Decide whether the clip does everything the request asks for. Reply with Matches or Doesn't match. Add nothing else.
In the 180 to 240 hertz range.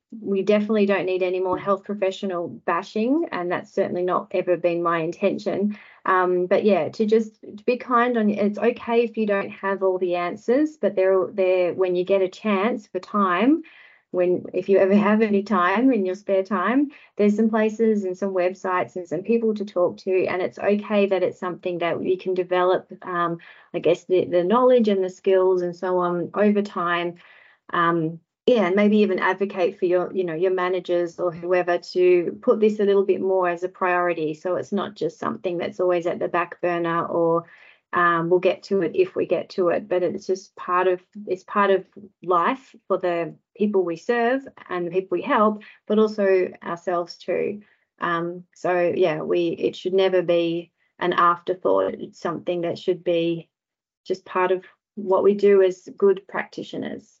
Matches